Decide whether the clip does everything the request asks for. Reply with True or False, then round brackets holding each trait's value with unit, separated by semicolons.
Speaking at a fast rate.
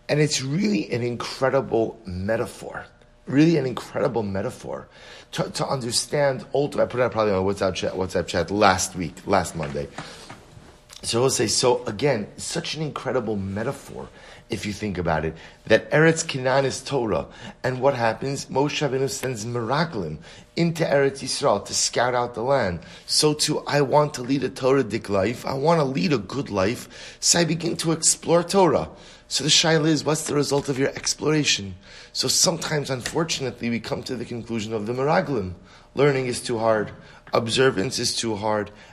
False (175 wpm)